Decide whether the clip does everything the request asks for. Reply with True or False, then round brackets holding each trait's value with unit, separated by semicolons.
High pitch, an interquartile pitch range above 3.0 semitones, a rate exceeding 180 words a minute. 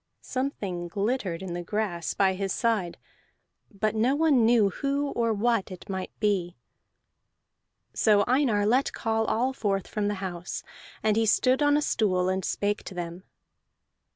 False (210 Hz; 4.0 semitones; 155 wpm)